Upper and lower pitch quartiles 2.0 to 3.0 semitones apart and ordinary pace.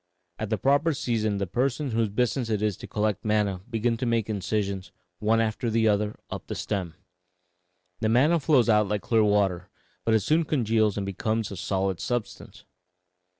Yes: narrow, 2.6 semitones; average, 180 wpm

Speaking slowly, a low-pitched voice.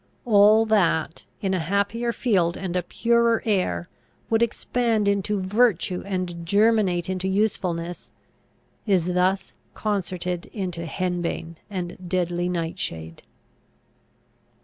No: slow, 105 wpm; medium, 185 Hz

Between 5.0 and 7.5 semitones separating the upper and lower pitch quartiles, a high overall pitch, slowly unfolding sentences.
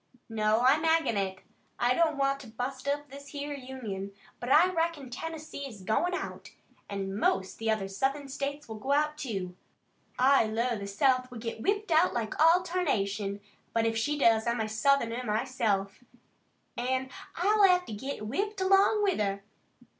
No: wide, 5.4 semitones; very high, 255 Hz; average, 175 wpm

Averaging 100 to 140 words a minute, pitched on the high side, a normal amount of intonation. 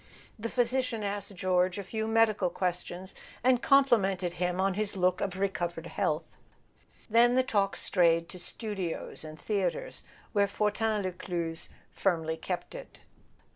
Yes: slow, 135 wpm; high, 195 Hz; average, 3.6 semitones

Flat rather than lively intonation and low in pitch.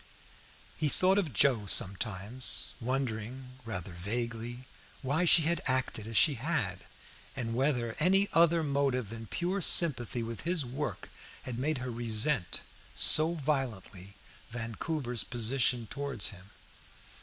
No: average, 4.7 semitones; low, 125 Hz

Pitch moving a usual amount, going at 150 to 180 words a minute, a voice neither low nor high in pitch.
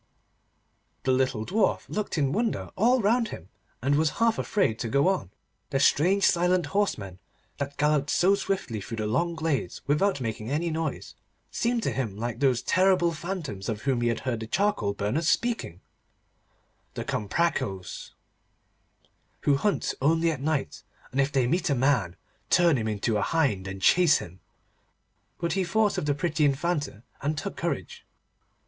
No: wide, 7.1 semitones; average, 165 wpm; medium, 145 Hz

